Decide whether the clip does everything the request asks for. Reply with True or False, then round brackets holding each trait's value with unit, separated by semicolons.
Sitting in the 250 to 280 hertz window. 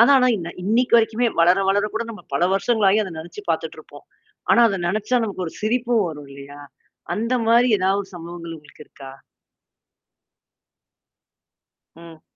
False (200 Hz)